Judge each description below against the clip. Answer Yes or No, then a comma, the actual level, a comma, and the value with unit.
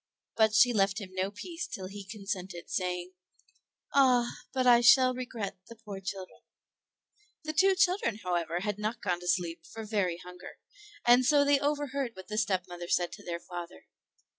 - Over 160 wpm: Yes, average, 170 wpm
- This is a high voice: Yes, high, 205 Hz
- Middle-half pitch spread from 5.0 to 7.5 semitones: Yes, wide, 5.4 semitones